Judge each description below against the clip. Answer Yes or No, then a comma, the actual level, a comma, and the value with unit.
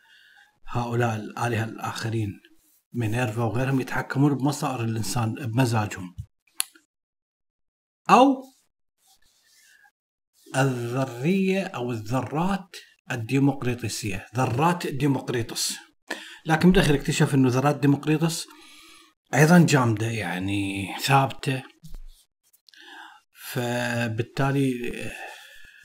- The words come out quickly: No, slow, 65 wpm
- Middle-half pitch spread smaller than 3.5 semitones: No, average, 4.7 semitones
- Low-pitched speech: Yes, low, 130 Hz